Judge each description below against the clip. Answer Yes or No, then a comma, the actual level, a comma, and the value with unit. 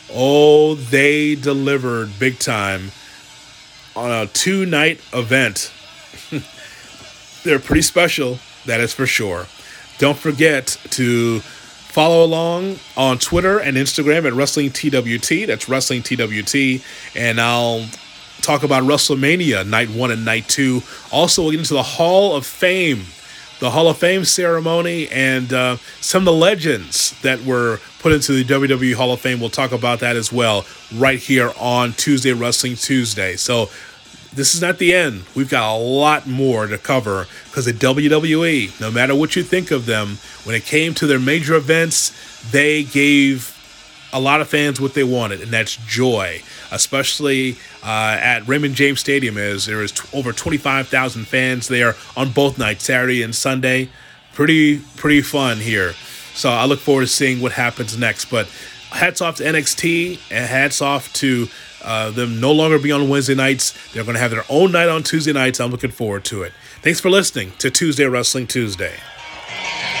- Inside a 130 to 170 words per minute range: Yes, average, 165 wpm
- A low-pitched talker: Yes, low, 130 Hz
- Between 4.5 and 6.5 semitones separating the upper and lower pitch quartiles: No, average, 3.7 semitones